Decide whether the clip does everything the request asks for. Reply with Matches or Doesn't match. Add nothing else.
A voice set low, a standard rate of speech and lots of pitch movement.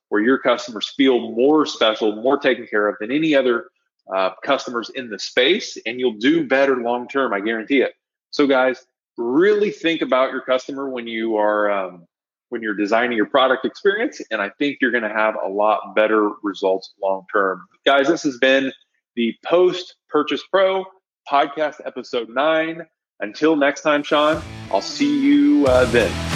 Matches